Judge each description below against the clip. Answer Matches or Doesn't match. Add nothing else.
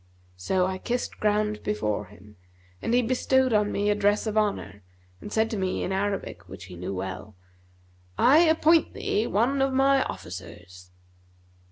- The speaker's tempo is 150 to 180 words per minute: Matches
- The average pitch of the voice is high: Matches